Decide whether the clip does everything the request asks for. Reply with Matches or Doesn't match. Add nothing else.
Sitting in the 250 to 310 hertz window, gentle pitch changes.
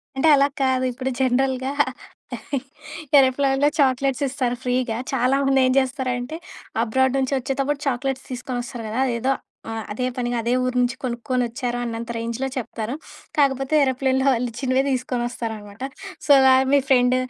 Matches